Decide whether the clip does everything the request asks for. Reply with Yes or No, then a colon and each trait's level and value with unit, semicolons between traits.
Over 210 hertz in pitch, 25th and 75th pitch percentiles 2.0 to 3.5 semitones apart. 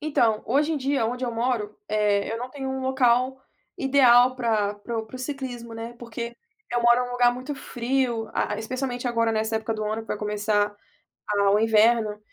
Yes: high, 235 Hz; average, 2.7 semitones